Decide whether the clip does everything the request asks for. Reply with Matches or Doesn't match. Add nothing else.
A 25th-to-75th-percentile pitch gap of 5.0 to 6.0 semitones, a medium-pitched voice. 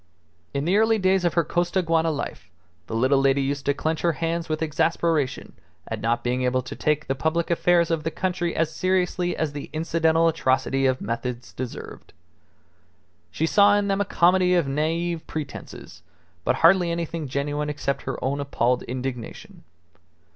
Doesn't match